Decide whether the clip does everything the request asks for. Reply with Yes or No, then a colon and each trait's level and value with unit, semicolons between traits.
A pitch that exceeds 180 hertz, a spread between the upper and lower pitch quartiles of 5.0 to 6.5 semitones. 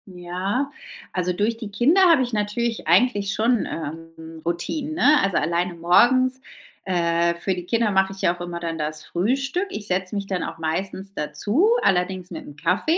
Yes: high, 190 Hz; wide, 5.4 semitones